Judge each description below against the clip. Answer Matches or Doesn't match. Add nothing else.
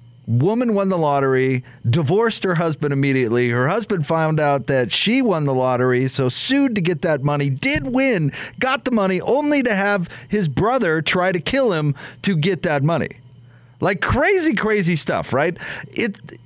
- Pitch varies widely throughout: Matches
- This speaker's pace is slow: Doesn't match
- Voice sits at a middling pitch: Matches